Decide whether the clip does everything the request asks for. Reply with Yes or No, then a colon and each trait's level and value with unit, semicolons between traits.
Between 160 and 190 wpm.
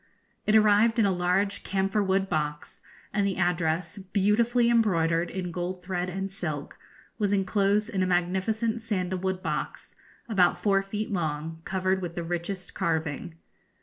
No: average, 150 wpm